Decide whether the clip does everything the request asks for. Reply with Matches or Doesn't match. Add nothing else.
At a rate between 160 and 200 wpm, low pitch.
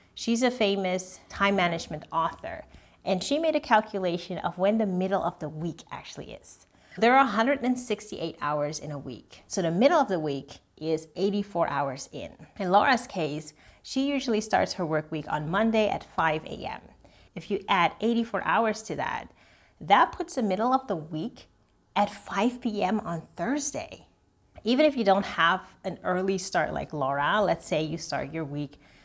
Doesn't match